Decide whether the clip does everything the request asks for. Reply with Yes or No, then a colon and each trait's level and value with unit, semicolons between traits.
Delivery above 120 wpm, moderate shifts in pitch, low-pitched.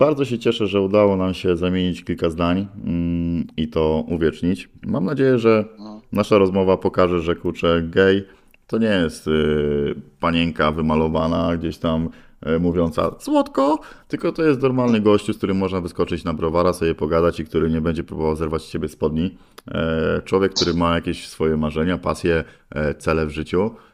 Yes: fast, 160 wpm; average, 3.3 semitones; very low, 85 Hz